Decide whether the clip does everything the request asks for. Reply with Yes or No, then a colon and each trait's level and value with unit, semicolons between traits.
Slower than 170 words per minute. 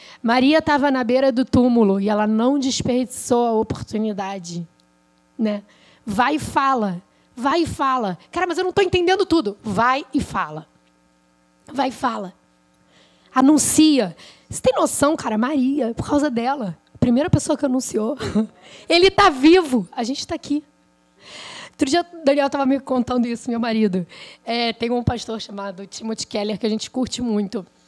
Yes: average, 160 wpm